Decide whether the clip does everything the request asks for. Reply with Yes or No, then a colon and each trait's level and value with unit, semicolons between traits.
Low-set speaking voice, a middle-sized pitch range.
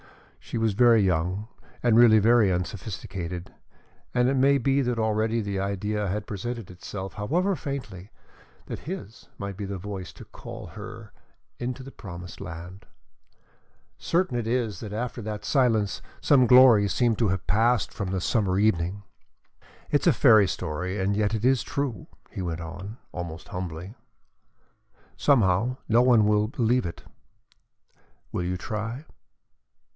Yes: low, 105 Hz; average, 4.2 semitones